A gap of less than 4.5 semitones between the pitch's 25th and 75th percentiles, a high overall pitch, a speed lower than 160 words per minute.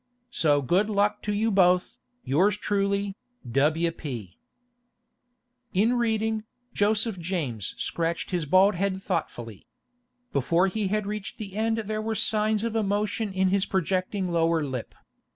Yes: average, 4.0 semitones; high, 195 Hz; average, 140 wpm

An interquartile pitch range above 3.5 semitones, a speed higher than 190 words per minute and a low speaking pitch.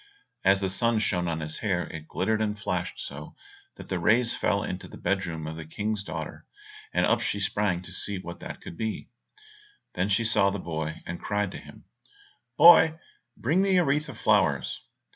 Yes: average, 4.2 semitones; average, 200 wpm; low, 100 Hz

